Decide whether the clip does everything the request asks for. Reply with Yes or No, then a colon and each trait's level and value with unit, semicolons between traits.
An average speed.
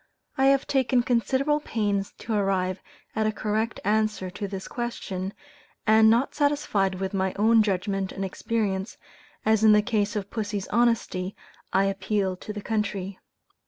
Yes: average, 155 wpm